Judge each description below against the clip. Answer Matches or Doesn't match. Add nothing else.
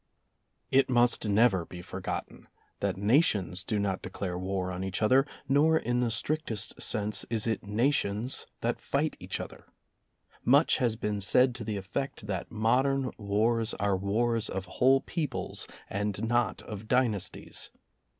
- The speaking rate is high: Doesn't match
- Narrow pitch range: Doesn't match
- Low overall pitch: Matches